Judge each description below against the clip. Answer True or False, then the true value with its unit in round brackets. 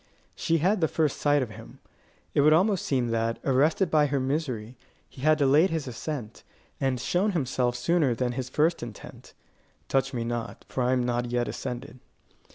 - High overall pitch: False (135 Hz)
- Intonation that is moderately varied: True (4.1 semitones)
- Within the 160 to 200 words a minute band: True (180 wpm)